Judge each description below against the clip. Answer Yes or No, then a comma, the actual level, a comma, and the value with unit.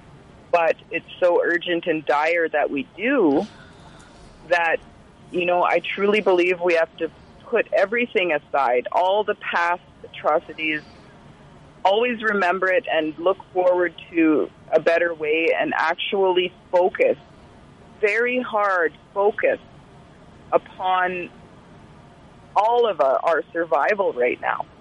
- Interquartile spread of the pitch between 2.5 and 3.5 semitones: No, average, 4.3 semitones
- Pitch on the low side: No, medium, 180 Hz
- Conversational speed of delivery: No, slow, 120 wpm